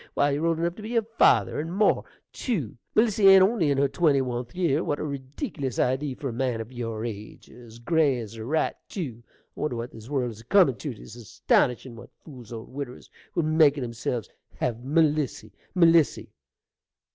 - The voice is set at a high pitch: No, low, 135 Hz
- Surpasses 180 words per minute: Yes, average, 200 wpm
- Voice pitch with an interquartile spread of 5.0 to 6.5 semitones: Yes, wide, 5.4 semitones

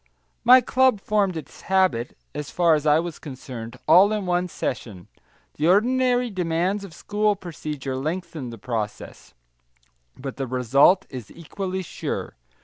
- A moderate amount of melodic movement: No, wide, 6.8 semitones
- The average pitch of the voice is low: No, medium, 170 Hz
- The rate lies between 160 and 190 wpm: No, average, 145 wpm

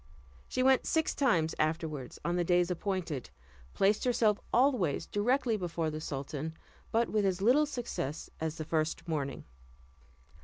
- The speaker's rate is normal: Yes, average, 145 wpm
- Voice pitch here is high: No, medium, 175 Hz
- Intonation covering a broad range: Yes, wide, 6.4 semitones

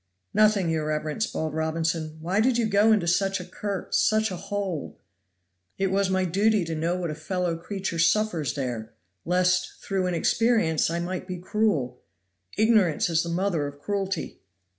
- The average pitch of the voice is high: No, medium, 180 Hz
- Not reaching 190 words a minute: Yes, average, 170 wpm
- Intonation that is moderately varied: Yes, average, 3.7 semitones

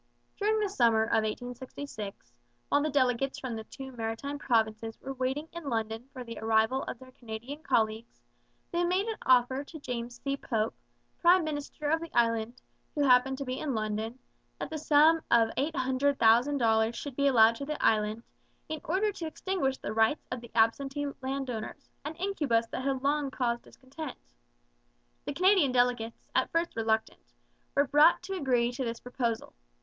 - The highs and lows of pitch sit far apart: No, average, 4.1 semitones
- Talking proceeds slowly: No, average, 170 wpm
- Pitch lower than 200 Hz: No, very high, 260 Hz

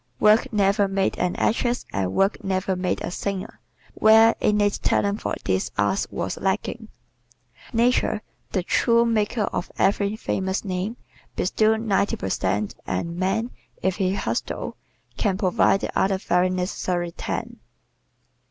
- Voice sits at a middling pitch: No, high, 195 Hz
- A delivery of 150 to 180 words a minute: No, average, 140 wpm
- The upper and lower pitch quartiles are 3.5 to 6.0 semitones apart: No, average, 2.8 semitones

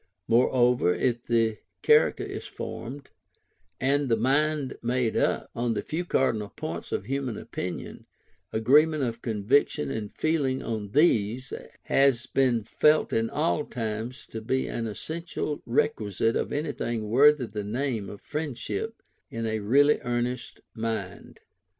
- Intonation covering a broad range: No, average, 4.0 semitones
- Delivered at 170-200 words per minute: No, slow, 135 wpm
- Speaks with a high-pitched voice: No, low, 120 Hz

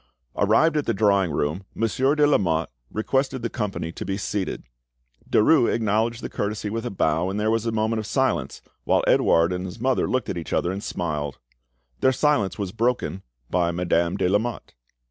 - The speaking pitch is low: Yes, low, 105 Hz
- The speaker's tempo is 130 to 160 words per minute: No, average, 185 wpm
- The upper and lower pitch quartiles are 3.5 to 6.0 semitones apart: Yes, average, 4.5 semitones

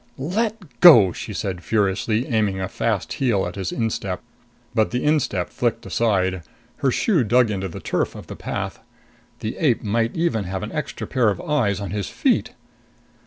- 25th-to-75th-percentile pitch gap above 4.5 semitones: Yes, average, 5.0 semitones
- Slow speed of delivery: No, average, 175 wpm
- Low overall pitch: Yes, low, 110 Hz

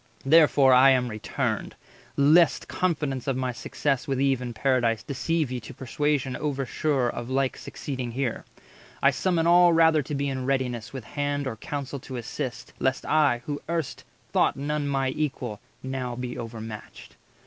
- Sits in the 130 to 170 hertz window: Yes, low, 135 Hz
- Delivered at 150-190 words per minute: Yes, average, 170 wpm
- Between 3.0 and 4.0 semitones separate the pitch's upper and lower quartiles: No, narrow, 2.6 semitones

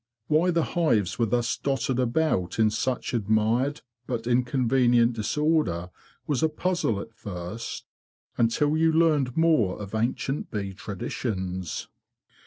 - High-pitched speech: No, low, 120 Hz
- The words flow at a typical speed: No, slow, 125 wpm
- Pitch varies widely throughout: Yes, wide, 5.7 semitones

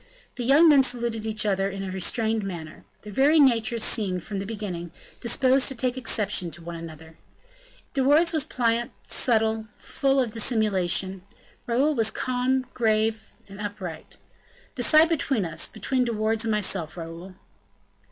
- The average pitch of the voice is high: Yes, high, 220 Hz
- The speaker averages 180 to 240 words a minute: No, average, 155 wpm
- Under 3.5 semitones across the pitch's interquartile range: No, average, 4.7 semitones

